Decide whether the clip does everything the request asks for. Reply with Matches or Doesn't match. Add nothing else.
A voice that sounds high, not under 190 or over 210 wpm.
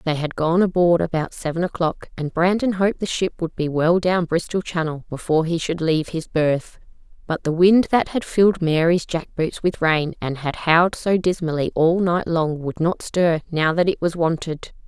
Doesn't match